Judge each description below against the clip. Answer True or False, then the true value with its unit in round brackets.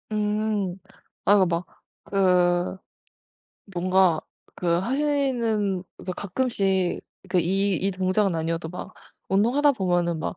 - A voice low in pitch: False (190 Hz)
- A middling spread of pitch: True (3.0 semitones)